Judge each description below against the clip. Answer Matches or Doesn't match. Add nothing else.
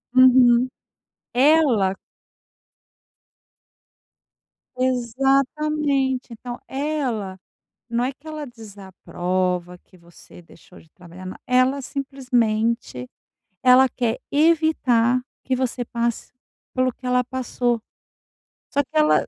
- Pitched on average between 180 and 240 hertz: Doesn't match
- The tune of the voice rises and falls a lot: Doesn't match